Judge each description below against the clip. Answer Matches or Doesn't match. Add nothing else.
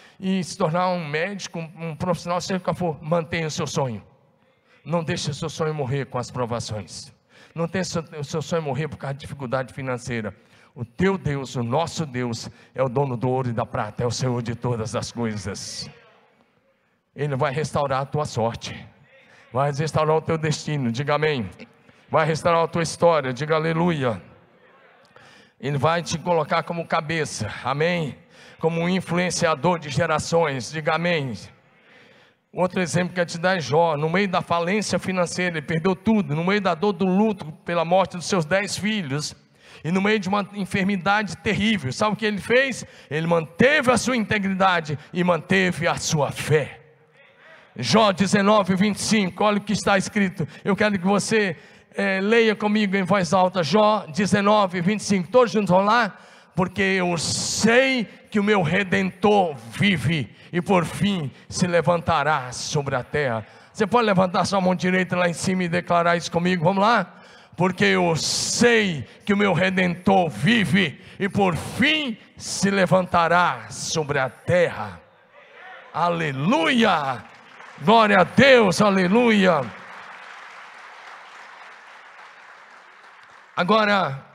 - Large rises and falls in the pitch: Doesn't match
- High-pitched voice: Doesn't match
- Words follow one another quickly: Doesn't match